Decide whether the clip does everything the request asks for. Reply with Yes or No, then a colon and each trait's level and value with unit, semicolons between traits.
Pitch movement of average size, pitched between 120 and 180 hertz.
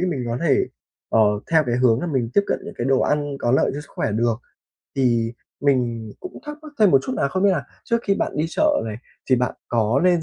No: wide, 7.0 semitones; low, 135 Hz